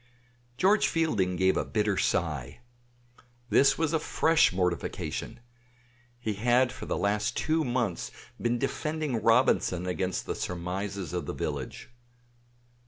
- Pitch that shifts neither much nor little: No, wide, 6.4 semitones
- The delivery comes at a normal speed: No, slow, 125 wpm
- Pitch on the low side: Yes, low, 105 Hz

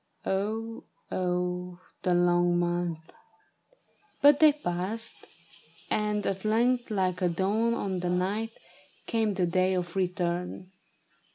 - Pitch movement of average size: Yes, average, 3.4 semitones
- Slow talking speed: Yes, slow, 115 wpm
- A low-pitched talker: No, medium, 185 Hz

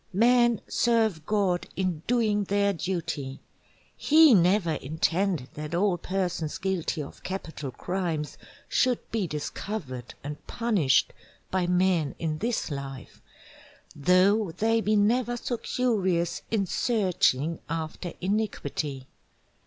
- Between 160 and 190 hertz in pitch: Yes, medium, 185 Hz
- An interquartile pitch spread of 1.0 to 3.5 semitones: No, average, 5.3 semitones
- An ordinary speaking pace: No, slow, 115 wpm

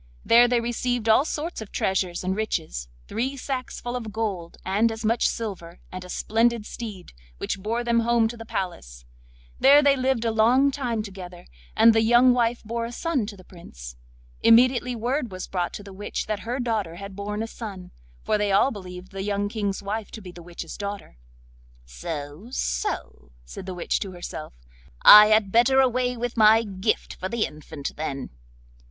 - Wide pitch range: No, average, 4.2 semitones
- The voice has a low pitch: No, high, 215 Hz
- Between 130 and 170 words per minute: No, average, 185 wpm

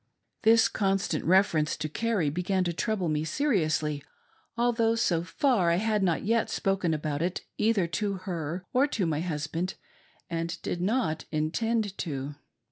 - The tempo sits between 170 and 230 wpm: No, average, 155 wpm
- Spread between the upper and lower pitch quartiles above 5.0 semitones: Yes, wide, 5.4 semitones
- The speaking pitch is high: No, medium, 180 Hz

